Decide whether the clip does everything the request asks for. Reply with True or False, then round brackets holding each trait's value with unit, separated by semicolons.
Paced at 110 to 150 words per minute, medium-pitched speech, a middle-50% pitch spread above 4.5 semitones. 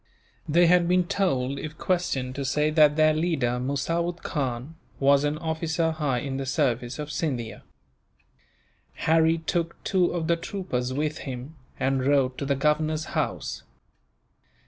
False (145 wpm; 150 Hz; 3.4 semitones)